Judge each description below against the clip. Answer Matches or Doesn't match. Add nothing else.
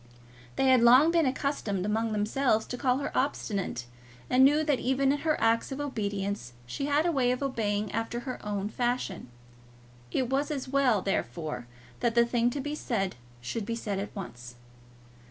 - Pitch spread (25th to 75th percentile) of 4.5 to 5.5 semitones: Matches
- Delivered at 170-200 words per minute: Matches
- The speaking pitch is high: Matches